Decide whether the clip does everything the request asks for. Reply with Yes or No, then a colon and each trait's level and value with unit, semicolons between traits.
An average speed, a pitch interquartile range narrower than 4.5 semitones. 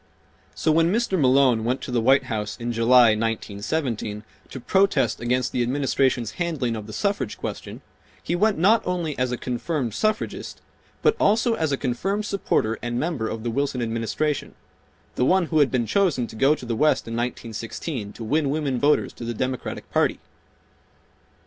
No: average, 175 wpm; wide, 5.5 semitones